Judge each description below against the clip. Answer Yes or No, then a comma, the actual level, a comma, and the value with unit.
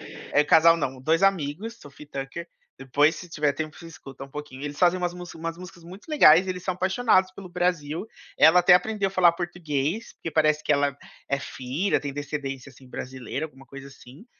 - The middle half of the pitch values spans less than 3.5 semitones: No, average, 4.0 semitones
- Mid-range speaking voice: Yes, medium, 160 Hz